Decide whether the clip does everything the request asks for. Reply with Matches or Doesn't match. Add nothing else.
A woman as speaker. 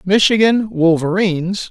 Doesn't match